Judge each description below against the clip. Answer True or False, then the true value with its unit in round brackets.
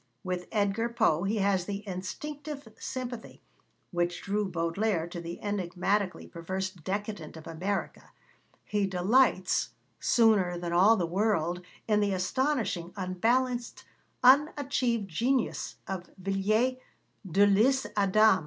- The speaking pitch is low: False (200 Hz)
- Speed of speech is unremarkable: False (115 wpm)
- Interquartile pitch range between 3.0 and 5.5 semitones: True (4.0 semitones)